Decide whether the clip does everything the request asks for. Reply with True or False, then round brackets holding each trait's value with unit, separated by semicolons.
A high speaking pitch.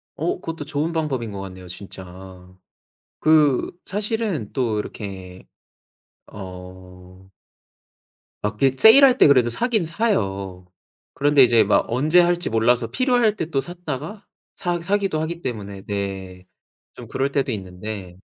False (125 Hz)